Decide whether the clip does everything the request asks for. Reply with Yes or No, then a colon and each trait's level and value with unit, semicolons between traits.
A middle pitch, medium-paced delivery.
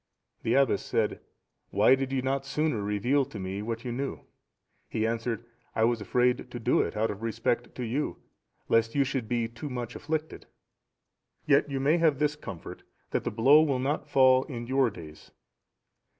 No: low, 125 Hz; average, 185 wpm